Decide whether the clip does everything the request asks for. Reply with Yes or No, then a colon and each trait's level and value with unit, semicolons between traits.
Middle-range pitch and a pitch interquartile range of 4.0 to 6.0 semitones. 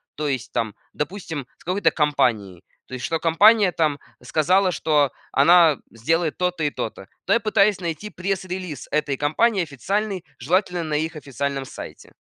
Yes: medium, 160 Hz; average, 4.5 semitones